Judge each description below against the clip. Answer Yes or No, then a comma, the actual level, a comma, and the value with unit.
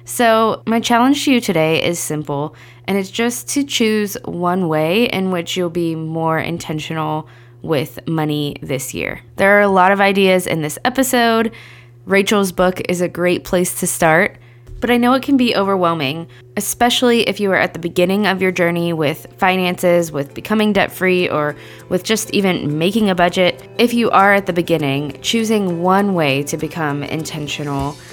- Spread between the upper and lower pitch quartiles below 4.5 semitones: No, average, 4.8 semitones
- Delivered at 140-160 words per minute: No, average, 180 wpm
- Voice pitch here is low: No, medium, 180 Hz